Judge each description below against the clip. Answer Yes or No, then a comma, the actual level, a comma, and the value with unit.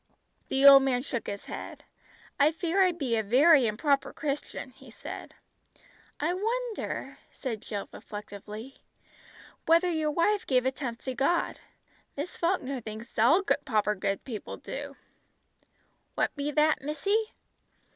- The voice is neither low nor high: No, very high, 275 Hz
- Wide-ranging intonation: Yes, wide, 6.1 semitones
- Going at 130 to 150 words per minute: Yes, slow, 135 wpm